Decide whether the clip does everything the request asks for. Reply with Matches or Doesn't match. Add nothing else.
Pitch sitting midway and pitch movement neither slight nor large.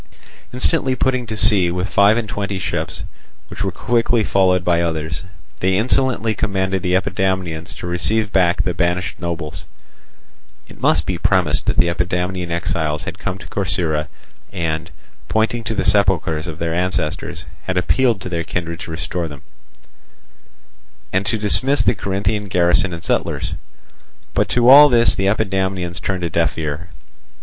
Doesn't match